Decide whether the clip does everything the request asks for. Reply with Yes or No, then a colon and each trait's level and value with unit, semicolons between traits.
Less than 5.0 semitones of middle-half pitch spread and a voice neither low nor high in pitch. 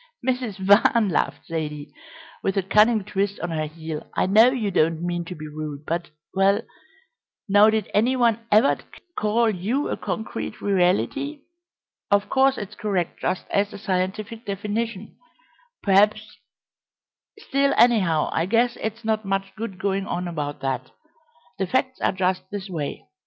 No: average, 3.6 semitones; high, 200 Hz